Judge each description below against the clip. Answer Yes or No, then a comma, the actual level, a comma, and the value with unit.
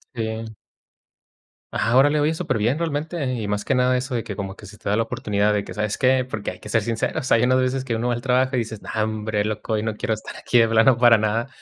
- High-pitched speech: No, low, 115 Hz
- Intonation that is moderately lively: Yes, average, 3.0 semitones